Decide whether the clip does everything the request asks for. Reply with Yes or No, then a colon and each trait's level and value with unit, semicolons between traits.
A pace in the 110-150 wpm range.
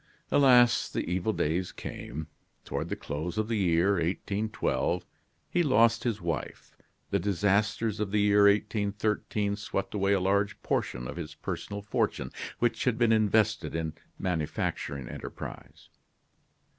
Yes: average, 140 wpm